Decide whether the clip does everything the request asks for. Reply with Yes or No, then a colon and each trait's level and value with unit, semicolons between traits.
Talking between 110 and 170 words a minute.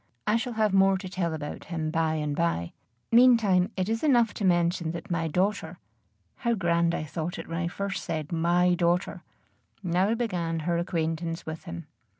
No: average, 180 wpm